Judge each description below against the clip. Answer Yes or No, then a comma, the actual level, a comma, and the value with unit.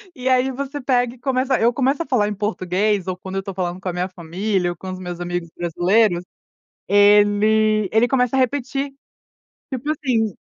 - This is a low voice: No, high, 215 Hz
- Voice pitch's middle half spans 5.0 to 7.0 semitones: Yes, wide, 5.5 semitones